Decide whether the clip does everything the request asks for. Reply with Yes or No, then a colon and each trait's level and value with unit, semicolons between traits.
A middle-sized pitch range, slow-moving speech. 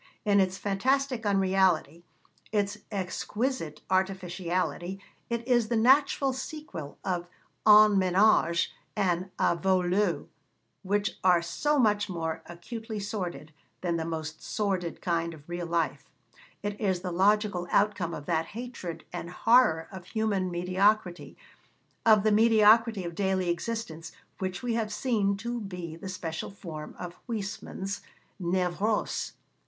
Yes: average, 3.6 semitones; slow, 130 wpm